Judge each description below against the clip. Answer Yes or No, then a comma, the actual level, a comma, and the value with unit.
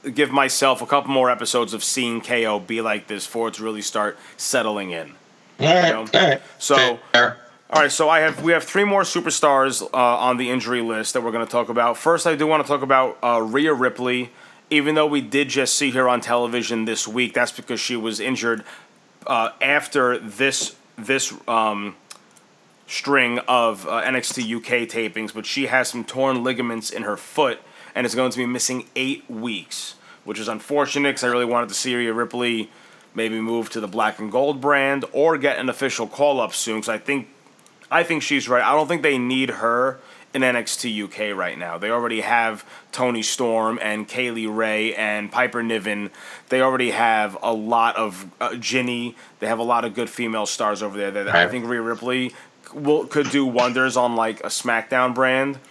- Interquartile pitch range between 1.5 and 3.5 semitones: Yes, average, 2.9 semitones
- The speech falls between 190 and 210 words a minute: Yes, average, 200 wpm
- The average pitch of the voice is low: Yes, low, 120 Hz